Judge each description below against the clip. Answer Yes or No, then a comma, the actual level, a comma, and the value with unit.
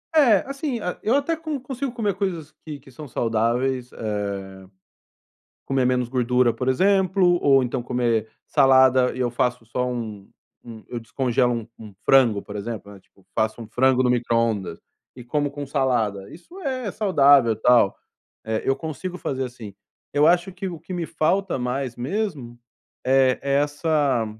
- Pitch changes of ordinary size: No, wide, 6.0 semitones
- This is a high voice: No, low, 130 Hz